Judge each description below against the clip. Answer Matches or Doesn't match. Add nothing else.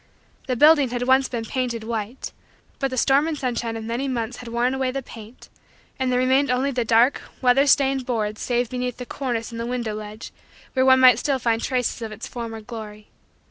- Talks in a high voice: Matches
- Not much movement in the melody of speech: Matches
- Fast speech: Matches